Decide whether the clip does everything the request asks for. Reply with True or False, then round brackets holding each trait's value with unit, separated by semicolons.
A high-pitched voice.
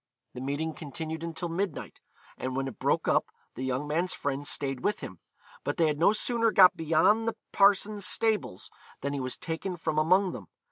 False (160 Hz)